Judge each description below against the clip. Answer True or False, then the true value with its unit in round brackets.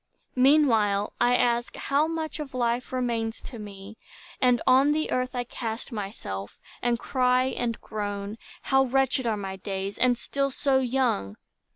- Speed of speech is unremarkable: True (155 wpm)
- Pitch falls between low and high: False (240 Hz)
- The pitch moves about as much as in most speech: True (3.9 semitones)